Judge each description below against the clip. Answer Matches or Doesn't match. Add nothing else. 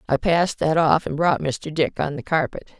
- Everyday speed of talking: Doesn't match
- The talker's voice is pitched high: Doesn't match